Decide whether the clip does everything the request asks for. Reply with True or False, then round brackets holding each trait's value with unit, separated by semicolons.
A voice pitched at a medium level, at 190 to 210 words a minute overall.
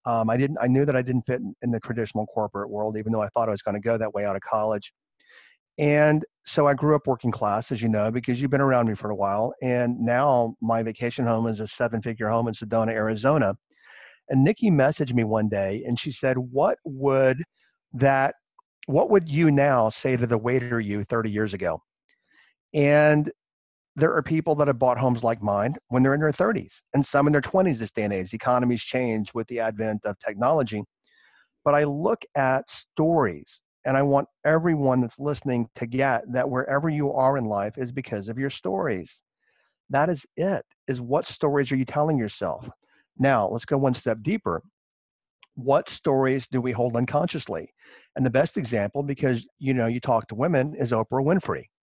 False (125 Hz; 200 wpm)